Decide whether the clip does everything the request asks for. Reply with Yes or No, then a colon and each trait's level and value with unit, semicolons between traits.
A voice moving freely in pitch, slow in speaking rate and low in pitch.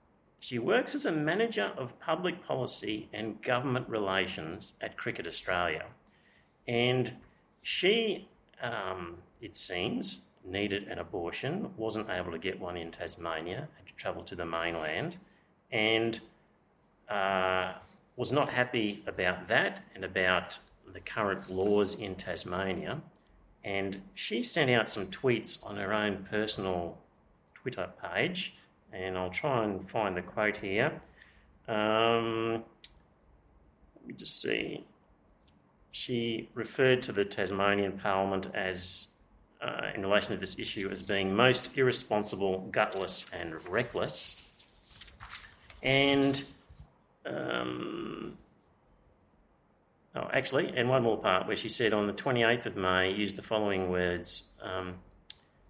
No: average, 3.8 semitones; slow, 125 wpm; low, 100 Hz